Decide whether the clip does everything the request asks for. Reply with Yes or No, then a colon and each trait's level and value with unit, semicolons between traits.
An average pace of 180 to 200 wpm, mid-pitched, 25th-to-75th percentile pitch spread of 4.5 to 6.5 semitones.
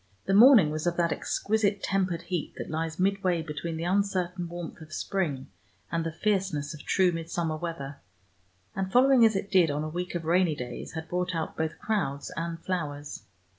No: average, 185 wpm; medium, 170 Hz; average, 3.3 semitones